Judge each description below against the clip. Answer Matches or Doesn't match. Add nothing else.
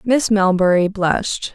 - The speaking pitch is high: Matches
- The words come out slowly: Matches